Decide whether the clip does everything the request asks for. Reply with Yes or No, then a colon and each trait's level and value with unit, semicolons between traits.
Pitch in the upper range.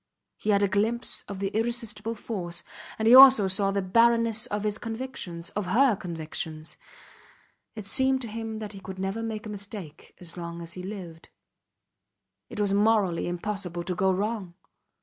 Yes: high, 205 Hz